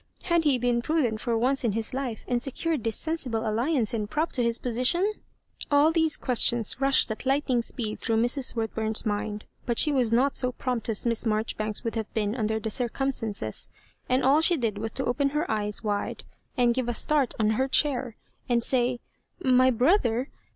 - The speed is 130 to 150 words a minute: No, fast, 205 wpm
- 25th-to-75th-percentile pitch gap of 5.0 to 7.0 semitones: No, average, 3.3 semitones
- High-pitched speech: Yes, high, 245 Hz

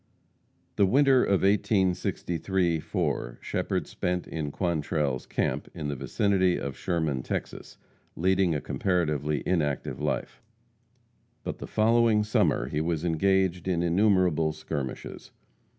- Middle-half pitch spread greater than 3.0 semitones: Yes, average, 3.9 semitones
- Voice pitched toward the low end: Yes, very low, 85 Hz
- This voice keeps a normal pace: No, slow, 120 wpm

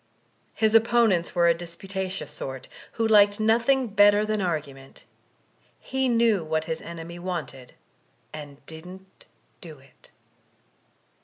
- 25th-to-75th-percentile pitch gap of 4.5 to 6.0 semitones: Yes, average, 5.1 semitones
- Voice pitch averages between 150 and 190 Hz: Yes, medium, 185 Hz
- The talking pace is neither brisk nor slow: No, slow, 120 wpm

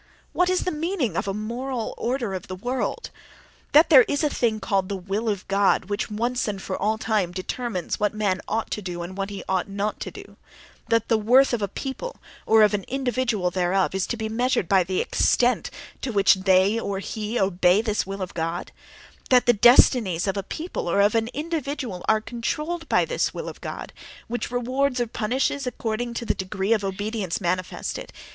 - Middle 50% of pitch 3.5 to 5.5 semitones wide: Yes, average, 4.3 semitones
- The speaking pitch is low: No, high, 215 Hz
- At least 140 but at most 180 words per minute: No, fast, 205 wpm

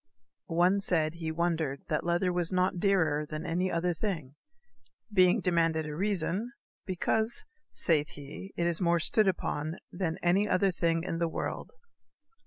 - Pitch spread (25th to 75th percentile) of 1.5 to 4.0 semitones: Yes, narrow, 2.5 semitones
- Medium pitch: Yes, medium, 170 Hz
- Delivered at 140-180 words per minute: Yes, average, 155 wpm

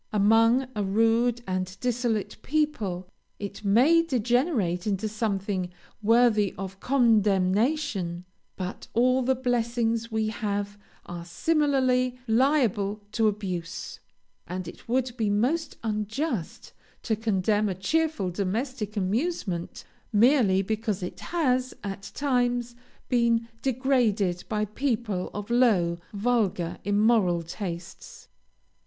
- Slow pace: Yes, slow, 110 wpm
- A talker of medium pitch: No, high, 220 Hz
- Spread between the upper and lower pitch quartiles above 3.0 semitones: Yes, average, 4.1 semitones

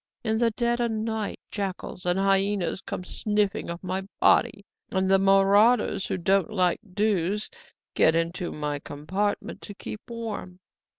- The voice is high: Yes, high, 195 Hz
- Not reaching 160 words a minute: Yes, average, 145 wpm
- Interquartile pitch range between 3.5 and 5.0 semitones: No, average, 2.8 semitones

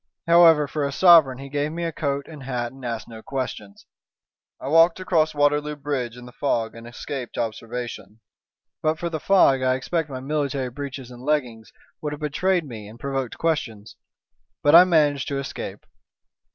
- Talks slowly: No, average, 180 wpm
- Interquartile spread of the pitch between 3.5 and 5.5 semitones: Yes, average, 3.9 semitones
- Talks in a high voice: No, medium, 140 Hz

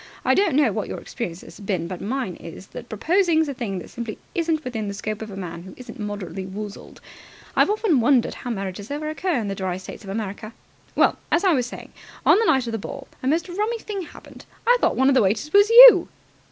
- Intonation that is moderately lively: No, wide, 8.0 semitones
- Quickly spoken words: Yes, fast, 235 wpm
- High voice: Yes, high, 235 Hz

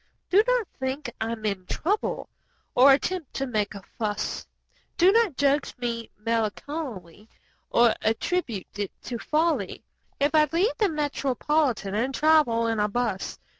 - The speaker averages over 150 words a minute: No, average, 145 wpm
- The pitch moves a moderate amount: No, wide, 6.0 semitones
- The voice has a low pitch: No, very high, 255 Hz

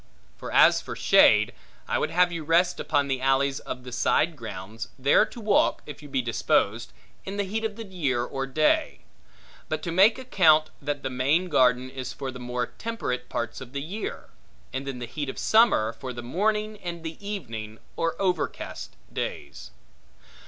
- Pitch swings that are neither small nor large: No, wide, 6.5 semitones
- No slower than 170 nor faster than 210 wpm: Yes, average, 185 wpm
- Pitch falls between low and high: Yes, medium, 145 Hz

